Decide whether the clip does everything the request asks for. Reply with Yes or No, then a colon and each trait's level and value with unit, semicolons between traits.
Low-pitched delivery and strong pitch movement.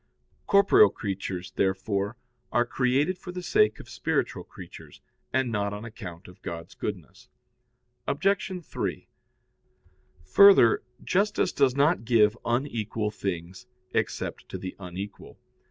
Yes: low, 115 Hz; wide, 7.1 semitones